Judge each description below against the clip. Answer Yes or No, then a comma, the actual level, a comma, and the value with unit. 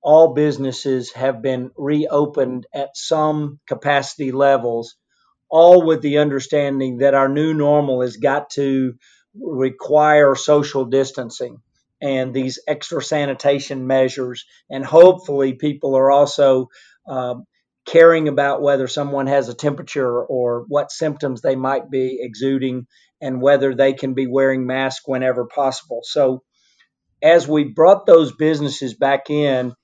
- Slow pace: Yes, slow, 130 wpm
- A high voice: No, medium, 140 Hz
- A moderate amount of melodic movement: No, narrow, 1.9 semitones